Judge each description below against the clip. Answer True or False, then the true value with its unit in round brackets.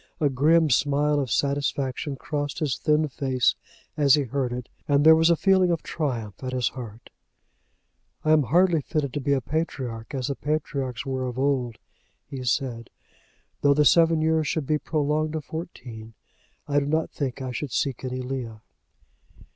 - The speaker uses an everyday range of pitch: True (3.2 semitones)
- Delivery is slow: False (175 wpm)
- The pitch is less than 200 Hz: True (140 Hz)